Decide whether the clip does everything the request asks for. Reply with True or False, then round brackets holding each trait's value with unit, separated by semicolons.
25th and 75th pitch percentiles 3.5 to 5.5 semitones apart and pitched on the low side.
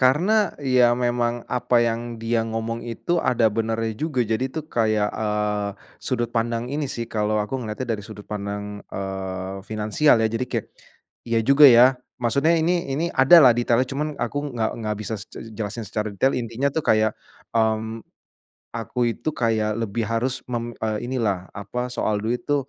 False (3.0 semitones; 115 Hz)